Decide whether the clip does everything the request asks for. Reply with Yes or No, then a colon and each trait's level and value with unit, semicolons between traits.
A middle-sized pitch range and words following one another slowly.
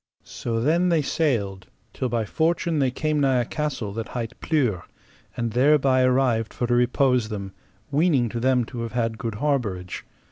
No: average, 4.0 semitones; average, 175 wpm